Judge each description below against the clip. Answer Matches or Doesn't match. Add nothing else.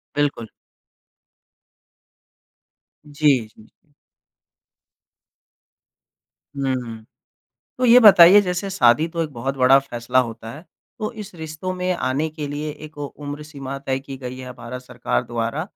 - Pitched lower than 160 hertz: Matches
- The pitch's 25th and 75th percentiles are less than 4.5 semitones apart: Matches